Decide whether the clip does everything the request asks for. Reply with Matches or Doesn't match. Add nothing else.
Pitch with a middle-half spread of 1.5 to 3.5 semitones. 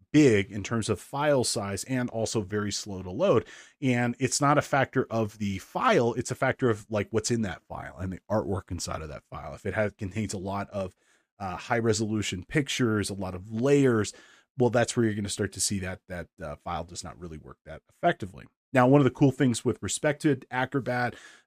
Doesn't match